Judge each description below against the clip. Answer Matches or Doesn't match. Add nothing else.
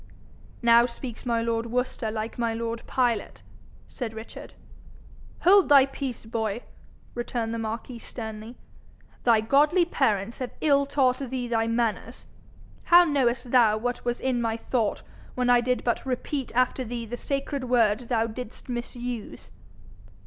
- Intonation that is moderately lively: Doesn't match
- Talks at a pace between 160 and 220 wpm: Doesn't match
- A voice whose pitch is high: Matches